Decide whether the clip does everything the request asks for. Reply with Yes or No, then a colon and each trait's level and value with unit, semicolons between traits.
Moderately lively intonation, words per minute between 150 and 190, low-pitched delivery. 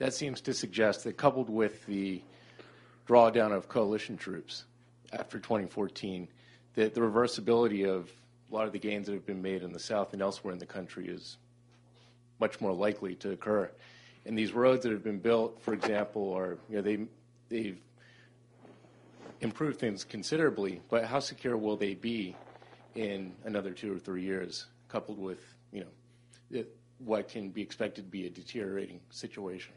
Yes: average, 3.2 semitones; average, 165 wpm; low, 110 Hz